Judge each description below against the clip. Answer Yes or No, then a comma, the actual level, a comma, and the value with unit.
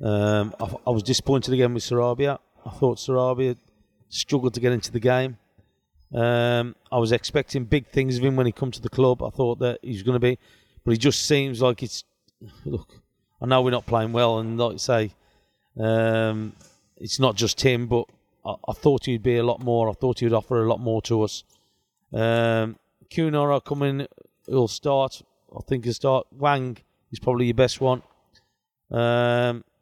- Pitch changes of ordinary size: No, narrow, 2.3 semitones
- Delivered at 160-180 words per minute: No, average, 195 wpm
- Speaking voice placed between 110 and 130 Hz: Yes, low, 120 Hz